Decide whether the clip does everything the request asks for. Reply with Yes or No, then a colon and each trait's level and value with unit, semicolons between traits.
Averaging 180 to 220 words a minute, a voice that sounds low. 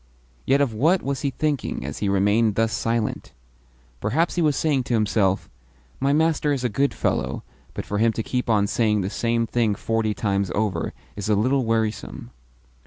Yes: average, 185 wpm; low, 115 Hz